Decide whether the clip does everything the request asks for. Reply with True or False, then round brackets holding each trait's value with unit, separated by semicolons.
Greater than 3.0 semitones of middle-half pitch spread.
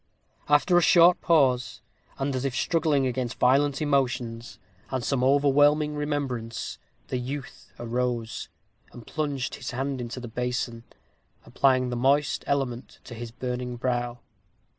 False (2.7 semitones)